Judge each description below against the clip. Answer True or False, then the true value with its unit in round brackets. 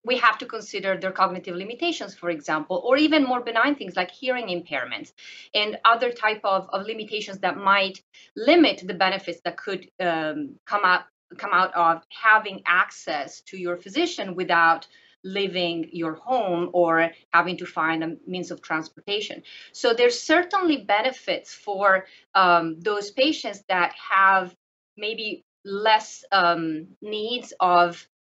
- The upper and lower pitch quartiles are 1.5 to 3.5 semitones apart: False (4.3 semitones)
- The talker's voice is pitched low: False (195 Hz)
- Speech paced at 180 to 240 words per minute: False (145 wpm)